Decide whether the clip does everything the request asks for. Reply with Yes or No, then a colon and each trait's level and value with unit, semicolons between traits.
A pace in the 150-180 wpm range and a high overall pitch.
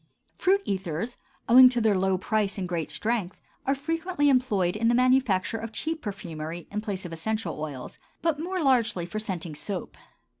Yes: average, 175 wpm; high, 215 Hz